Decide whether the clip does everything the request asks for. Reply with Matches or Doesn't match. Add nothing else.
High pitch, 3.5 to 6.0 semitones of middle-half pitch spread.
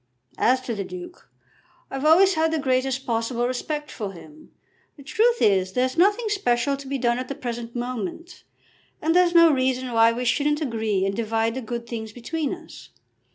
Matches